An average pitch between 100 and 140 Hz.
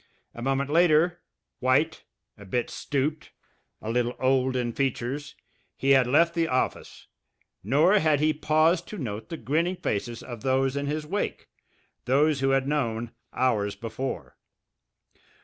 Yes: low, 135 Hz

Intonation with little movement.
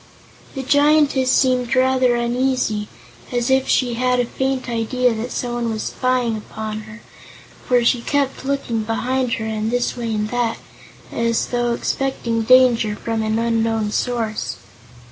Yes: narrow, 2.2 semitones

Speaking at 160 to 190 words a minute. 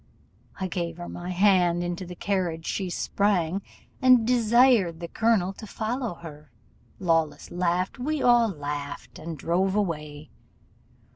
No: slow, 135 wpm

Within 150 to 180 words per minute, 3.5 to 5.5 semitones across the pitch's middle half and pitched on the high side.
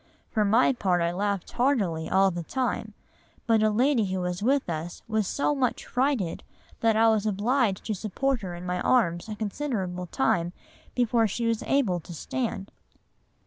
Yes: average, 175 wpm; average, 5.2 semitones; high, 210 Hz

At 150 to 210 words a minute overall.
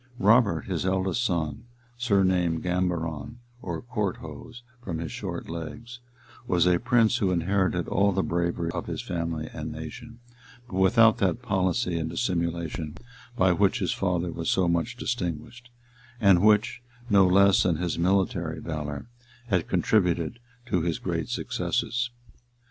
No: average, 140 wpm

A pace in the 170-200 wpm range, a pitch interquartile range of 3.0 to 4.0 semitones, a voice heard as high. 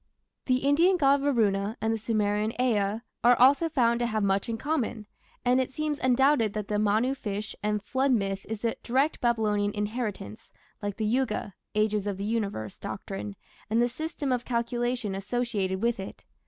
Yes: average, 175 wpm; average, 3.6 semitones; high, 225 Hz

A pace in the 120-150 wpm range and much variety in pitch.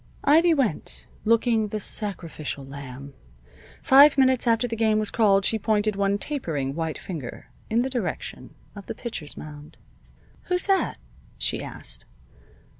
Yes: average, 140 wpm; wide, 7.2 semitones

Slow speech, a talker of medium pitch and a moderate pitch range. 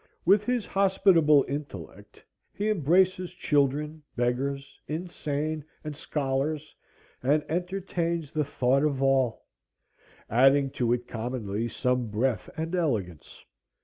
Yes: slow, 110 wpm; medium, 145 Hz; average, 4.4 semitones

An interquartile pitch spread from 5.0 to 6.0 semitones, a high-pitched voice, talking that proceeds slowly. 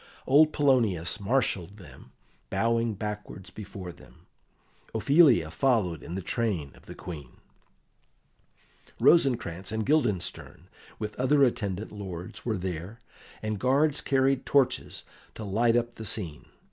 No: wide, 5.6 semitones; low, 110 Hz; slow, 120 wpm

